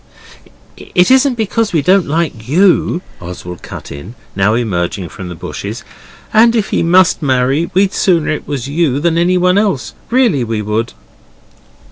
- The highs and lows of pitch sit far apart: Yes, wide, 8.6 semitones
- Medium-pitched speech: Yes, medium, 160 Hz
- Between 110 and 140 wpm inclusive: No, average, 150 wpm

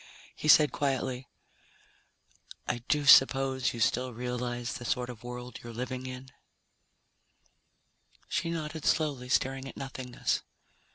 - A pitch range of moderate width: No, narrow, 1.6 semitones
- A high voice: No, low, 130 Hz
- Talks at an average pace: No, slow, 120 wpm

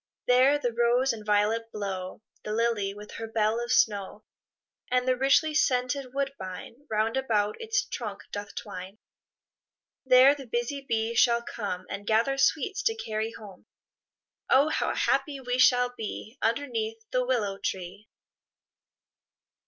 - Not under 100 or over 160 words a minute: Yes, average, 140 wpm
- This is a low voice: No, high, 235 Hz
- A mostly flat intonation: No, average, 3.7 semitones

